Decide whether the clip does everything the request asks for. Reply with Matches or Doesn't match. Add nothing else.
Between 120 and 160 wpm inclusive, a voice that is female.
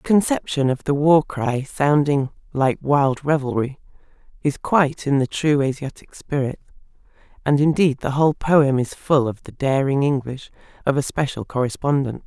Matches